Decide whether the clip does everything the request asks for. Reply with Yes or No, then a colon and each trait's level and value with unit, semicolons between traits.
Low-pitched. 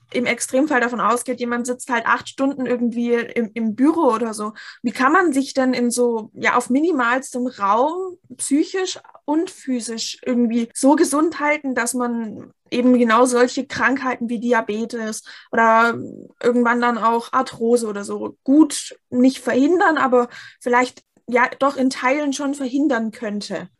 No: high, 245 Hz